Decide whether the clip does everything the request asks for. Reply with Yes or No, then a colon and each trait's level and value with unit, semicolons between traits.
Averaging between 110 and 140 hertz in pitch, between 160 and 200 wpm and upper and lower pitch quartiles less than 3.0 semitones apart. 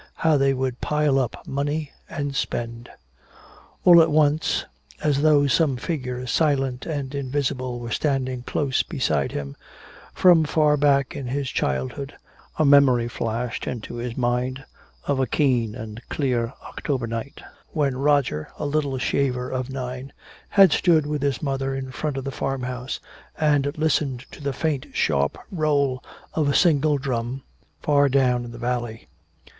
No: low, 135 Hz; average, 150 wpm; narrow, 2.6 semitones